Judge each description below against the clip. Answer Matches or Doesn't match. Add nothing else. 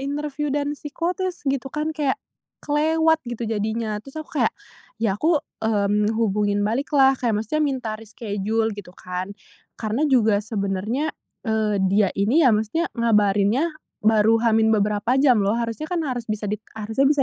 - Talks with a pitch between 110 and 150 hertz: Doesn't match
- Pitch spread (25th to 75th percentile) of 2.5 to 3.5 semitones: Doesn't match